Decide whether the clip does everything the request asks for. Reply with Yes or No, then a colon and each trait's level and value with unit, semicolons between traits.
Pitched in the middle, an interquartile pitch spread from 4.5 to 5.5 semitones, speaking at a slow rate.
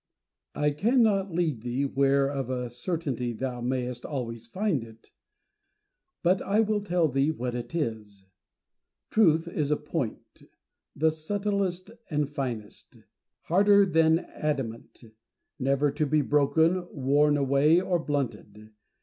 Yes: medium, 145 Hz; average, 5.2 semitones; slow, 130 wpm